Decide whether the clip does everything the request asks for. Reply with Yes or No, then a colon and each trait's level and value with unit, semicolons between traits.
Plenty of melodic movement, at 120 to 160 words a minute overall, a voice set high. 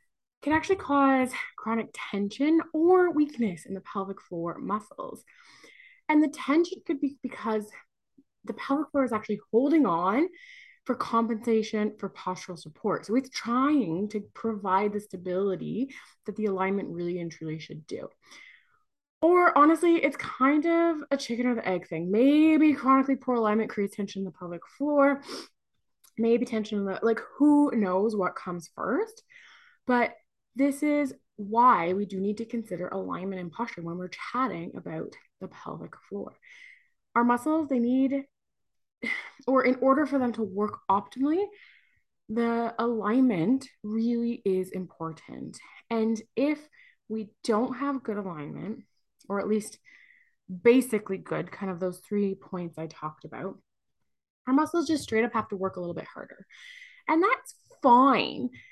Yes: wide, 6.6 semitones; average, 150 wpm; high, 235 Hz